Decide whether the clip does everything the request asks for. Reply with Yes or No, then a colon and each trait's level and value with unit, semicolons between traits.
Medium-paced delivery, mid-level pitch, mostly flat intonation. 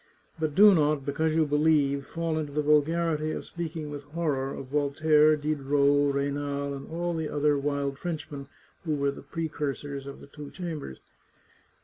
Yes: average, 160 wpm; medium, 150 Hz; narrow, 2.0 semitones